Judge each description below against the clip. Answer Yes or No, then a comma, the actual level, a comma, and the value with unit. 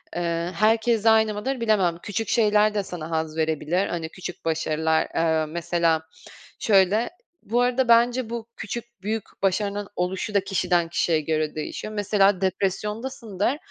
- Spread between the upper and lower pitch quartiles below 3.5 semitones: No, average, 4.8 semitones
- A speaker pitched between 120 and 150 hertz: No, high, 195 Hz